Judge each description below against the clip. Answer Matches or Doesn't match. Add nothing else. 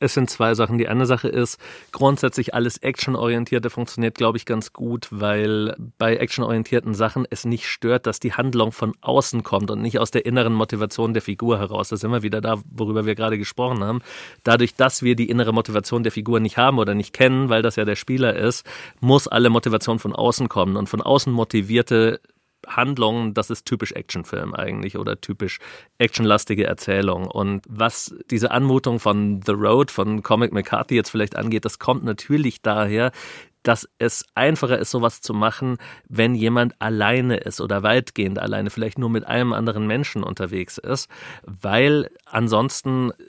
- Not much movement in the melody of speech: Matches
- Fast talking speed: Doesn't match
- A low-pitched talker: Matches